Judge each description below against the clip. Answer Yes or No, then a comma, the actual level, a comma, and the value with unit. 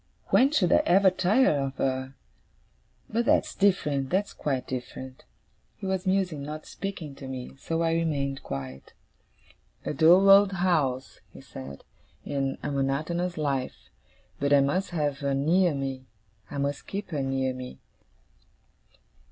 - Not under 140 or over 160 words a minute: Yes, average, 145 wpm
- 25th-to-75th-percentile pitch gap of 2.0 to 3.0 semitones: No, average, 5.2 semitones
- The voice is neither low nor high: Yes, medium, 145 Hz